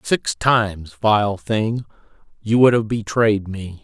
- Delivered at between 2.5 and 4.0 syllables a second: Yes, 3.5 syllables/s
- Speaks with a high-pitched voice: No, low, 110 Hz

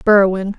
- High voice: Yes, high, 195 Hz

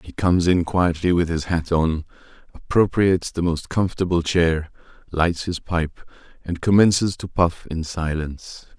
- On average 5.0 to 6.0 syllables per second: No, 4.7 syllables/s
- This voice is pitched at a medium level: No, very low, 85 Hz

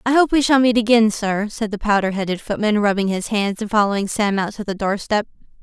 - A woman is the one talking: Yes, female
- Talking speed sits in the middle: No, fast, 245 wpm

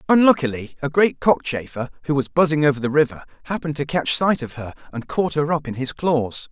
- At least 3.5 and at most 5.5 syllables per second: No, 5.9 syllables/s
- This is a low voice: No, medium, 145 Hz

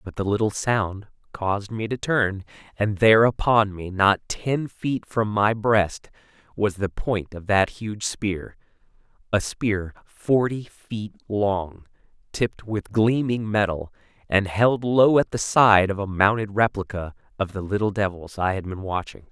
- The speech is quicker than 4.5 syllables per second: No, 4.1 syllables/s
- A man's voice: Yes, male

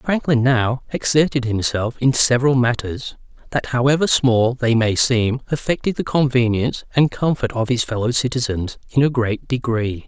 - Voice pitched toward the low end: Yes, low, 125 Hz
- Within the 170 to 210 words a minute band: No, average, 155 wpm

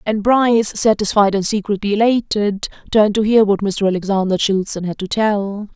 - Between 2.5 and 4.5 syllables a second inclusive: No, 5.4 syllables/s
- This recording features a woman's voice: Yes, female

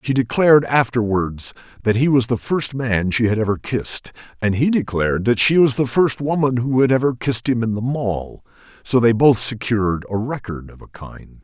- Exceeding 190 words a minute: Yes, fast, 205 wpm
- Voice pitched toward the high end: No, low, 120 Hz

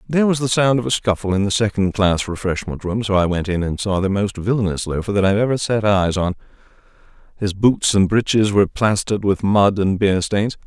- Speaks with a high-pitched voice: No, low, 100 Hz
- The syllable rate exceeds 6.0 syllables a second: No, 5.6 syllables/s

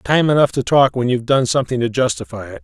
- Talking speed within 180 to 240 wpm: No, fast, 250 wpm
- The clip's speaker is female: No, male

